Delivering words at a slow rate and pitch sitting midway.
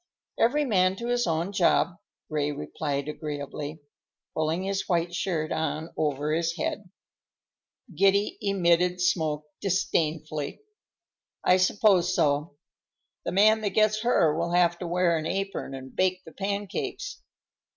Yes: slow, 130 wpm; medium, 175 Hz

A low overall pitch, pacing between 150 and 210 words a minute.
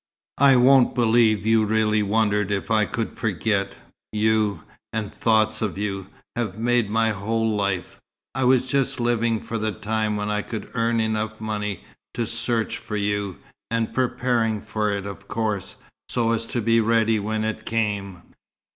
Yes: low, 110 Hz; average, 165 wpm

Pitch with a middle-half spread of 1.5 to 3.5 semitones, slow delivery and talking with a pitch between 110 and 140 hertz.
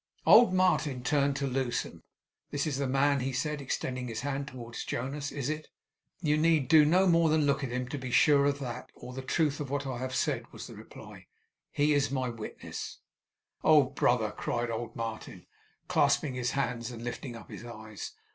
No: average, 2.9 semitones; average, 200 wpm; low, 135 Hz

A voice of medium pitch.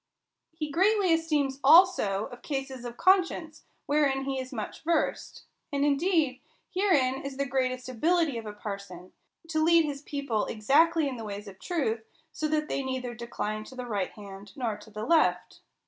No: very high, 270 Hz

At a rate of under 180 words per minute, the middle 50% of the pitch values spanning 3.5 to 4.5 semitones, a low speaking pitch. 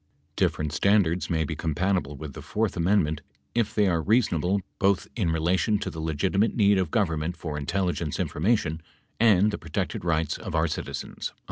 Yes: average, 170 wpm; average, 4.1 semitones; very low, 85 Hz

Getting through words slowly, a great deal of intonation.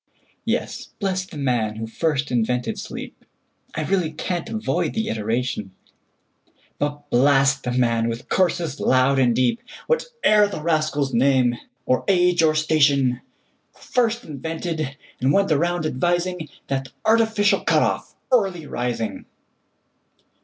Yes: slow, 115 wpm; wide, 6.0 semitones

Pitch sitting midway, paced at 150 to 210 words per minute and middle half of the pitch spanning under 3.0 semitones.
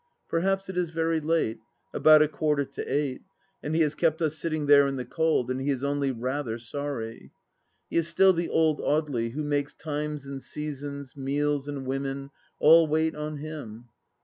Yes: medium, 145 Hz; average, 195 wpm; narrow, 2.5 semitones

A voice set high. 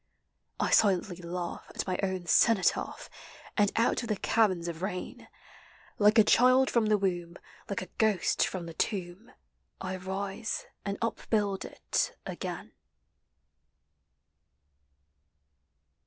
Yes: high, 195 Hz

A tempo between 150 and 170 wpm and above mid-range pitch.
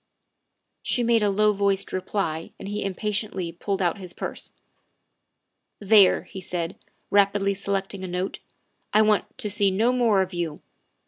Yes: average, 160 wpm; high, 195 Hz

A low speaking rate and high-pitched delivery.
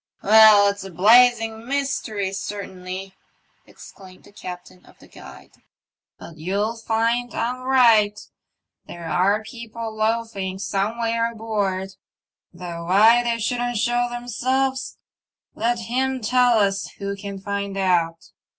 Yes: slow, 125 wpm; high, 215 Hz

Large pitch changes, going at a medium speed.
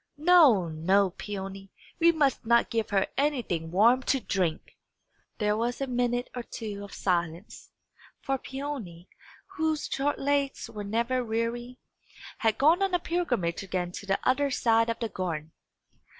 Yes: wide, 5.8 semitones; average, 150 wpm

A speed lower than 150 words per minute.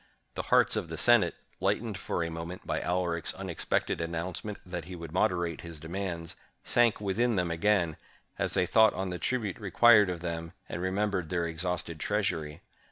No: average, 170 wpm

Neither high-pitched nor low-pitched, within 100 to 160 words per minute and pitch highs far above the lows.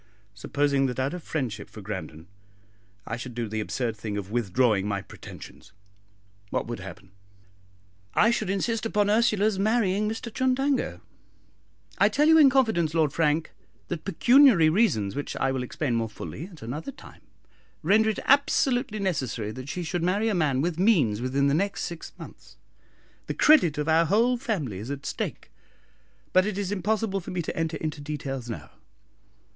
No: medium, 160 Hz; average, 170 wpm; wide, 9.0 semitones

